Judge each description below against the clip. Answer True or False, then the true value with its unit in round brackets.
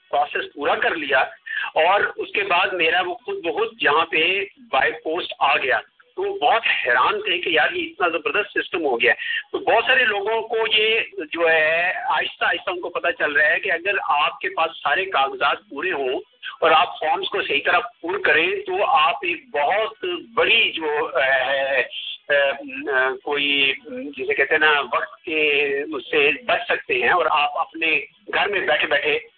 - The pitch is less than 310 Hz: False (385 Hz)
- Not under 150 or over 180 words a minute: False (190 wpm)